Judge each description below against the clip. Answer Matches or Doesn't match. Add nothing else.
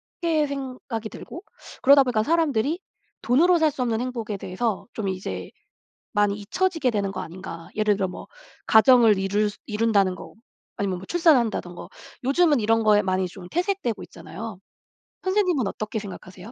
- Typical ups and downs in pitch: Doesn't match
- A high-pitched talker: Matches